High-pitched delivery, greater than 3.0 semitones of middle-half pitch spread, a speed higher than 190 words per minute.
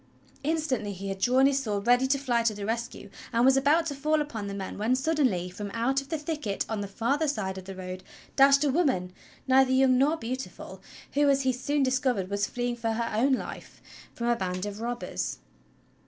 Yes: high, 245 Hz; average, 5.1 semitones; fast, 205 wpm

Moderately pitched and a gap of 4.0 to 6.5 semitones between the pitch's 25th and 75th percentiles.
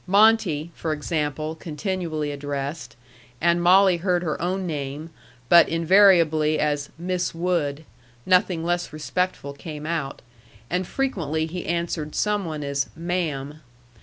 No: medium, 165 Hz; average, 3.1 semitones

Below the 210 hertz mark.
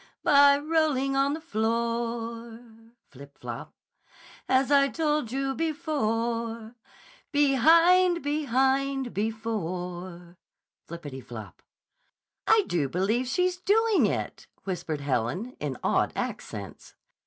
No: high, 235 Hz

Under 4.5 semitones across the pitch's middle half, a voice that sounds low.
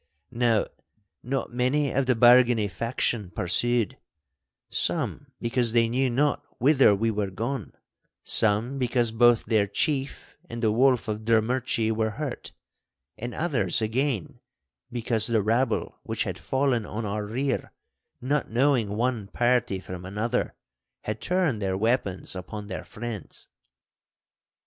Yes: average, 3.0 semitones; low, 115 Hz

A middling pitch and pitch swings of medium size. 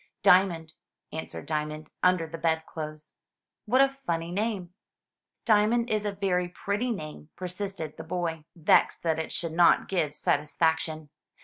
Yes: medium, 170 Hz; average, 3.8 semitones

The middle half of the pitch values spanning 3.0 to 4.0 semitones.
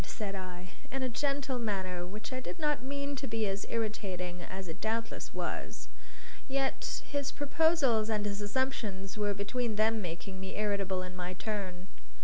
No: average, 5.3 semitones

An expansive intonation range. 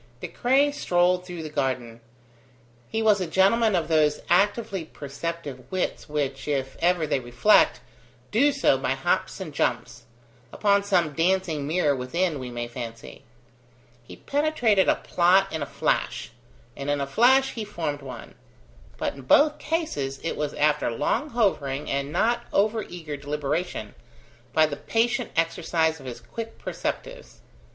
Yes: wide, 6.5 semitones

